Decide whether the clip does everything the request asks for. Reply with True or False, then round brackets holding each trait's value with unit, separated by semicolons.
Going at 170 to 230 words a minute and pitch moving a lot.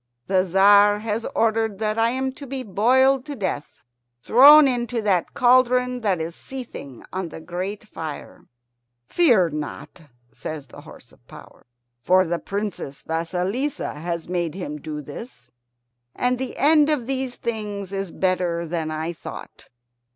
False (150 wpm; 6.7 semitones)